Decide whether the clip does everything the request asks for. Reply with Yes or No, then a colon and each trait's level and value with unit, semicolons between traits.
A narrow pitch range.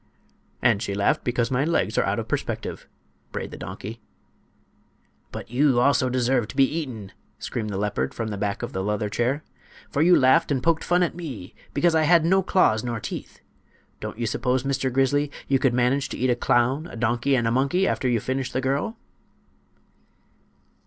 No: average, 3.7 semitones